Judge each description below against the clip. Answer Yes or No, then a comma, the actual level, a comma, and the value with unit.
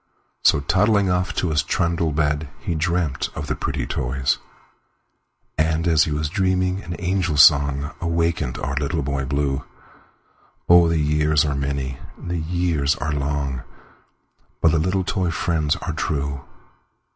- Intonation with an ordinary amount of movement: Yes, average, 3.4 semitones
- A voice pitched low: Yes, very low, 75 Hz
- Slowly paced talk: Yes, slow, 130 wpm